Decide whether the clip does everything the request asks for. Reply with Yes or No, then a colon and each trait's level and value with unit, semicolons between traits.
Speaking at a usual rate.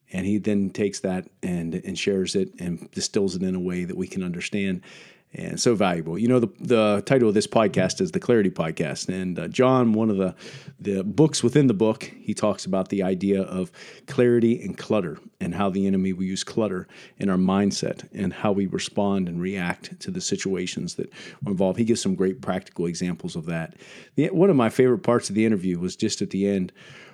No: fast, 215 wpm